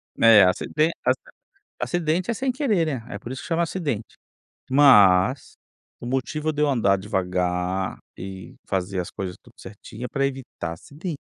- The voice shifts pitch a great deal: Yes, wide, 8.2 semitones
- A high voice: No, low, 120 Hz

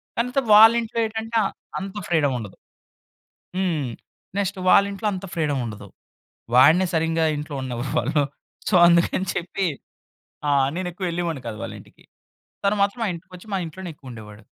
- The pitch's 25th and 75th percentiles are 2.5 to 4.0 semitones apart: No, average, 5.3 semitones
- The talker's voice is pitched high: No, medium, 170 Hz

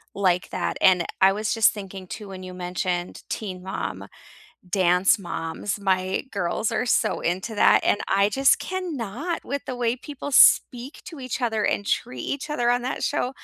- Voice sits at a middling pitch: No, high, 205 Hz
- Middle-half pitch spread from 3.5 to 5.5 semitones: Yes, average, 5.1 semitones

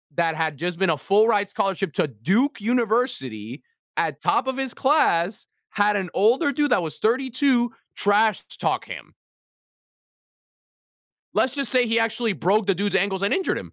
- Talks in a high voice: Yes, high, 210 Hz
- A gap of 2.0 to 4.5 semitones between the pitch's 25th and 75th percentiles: No, average, 5.3 semitones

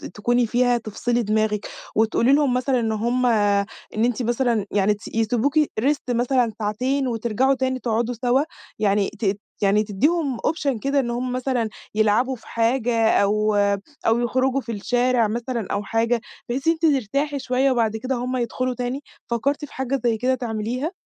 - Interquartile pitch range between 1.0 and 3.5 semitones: Yes, average, 2.9 semitones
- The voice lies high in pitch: Yes, high, 240 Hz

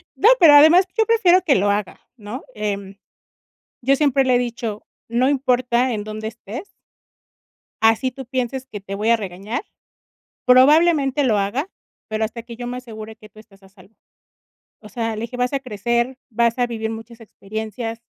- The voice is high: Yes, high, 235 Hz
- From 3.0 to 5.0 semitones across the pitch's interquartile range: Yes, average, 3.3 semitones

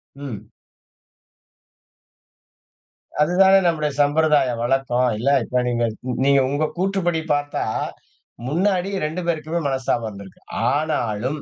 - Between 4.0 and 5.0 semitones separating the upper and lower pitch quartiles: Yes, average, 4.7 semitones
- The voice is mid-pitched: Yes, medium, 145 Hz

